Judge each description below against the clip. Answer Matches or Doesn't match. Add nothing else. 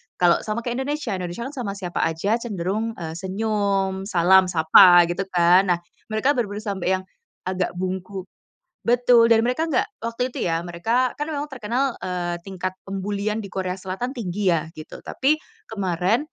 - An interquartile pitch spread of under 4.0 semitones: Doesn't match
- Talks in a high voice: Matches